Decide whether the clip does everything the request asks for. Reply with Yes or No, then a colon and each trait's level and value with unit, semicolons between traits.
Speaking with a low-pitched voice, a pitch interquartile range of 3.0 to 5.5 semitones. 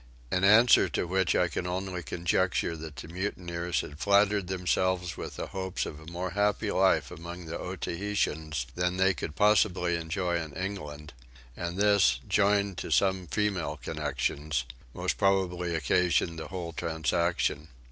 No: very low, 90 Hz; narrow, 2.6 semitones